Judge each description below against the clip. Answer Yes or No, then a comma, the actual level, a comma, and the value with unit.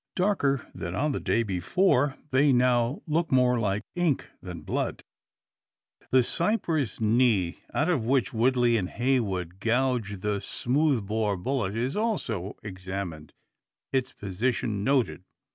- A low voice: Yes, low, 120 Hz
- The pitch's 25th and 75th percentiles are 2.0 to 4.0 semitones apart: No, average, 5.2 semitones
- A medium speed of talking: No, slow, 130 wpm